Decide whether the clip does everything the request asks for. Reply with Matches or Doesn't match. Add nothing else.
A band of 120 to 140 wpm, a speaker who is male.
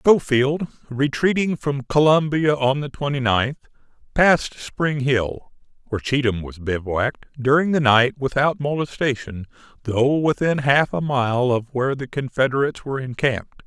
Matches